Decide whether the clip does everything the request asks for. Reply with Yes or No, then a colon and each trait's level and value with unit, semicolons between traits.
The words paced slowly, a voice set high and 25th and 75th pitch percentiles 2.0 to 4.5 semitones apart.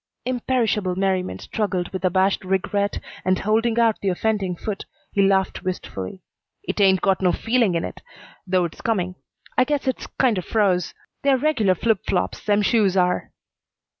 No: average, 160 wpm; high, 195 Hz; average, 3.3 semitones